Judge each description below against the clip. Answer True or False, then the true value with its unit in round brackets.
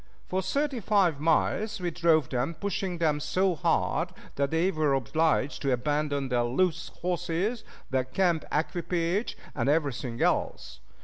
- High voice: False (165 Hz)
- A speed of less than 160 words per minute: True (140 wpm)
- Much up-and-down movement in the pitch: False (4.3 semitones)